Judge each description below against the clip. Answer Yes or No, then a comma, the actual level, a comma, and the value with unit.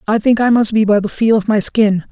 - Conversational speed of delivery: No, fast, 315 wpm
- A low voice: No, high, 215 Hz